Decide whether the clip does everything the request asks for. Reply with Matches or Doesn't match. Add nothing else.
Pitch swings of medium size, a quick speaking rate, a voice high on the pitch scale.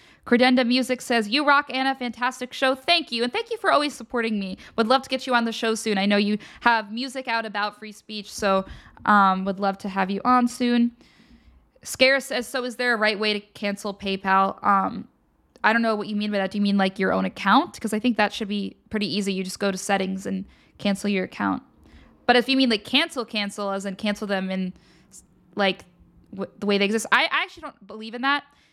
Matches